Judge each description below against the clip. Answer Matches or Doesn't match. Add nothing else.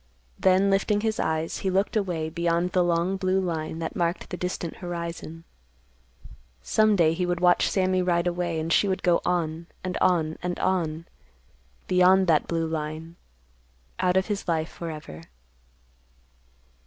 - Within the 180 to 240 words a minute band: Doesn't match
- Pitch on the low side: Doesn't match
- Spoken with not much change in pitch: Matches